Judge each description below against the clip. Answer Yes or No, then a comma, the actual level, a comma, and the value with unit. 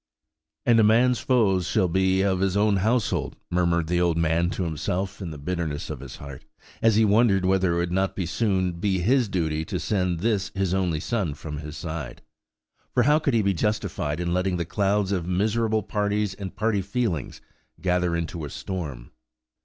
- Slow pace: No, average, 190 wpm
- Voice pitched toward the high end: No, very low, 95 Hz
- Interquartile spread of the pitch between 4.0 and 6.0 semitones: No, average, 3.6 semitones